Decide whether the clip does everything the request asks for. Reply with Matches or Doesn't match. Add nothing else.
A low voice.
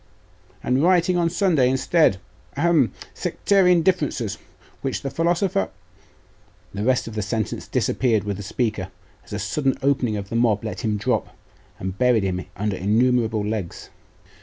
Matches